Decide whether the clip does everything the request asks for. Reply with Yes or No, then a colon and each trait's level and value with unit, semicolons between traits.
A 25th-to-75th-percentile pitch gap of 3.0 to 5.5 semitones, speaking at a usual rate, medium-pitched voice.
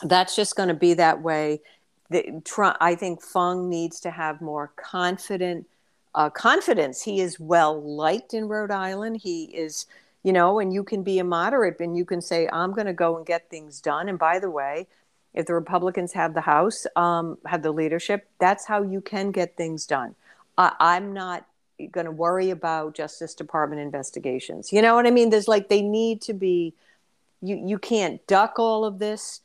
Yes: average, 3.4 semitones; average, 195 wpm; medium, 175 Hz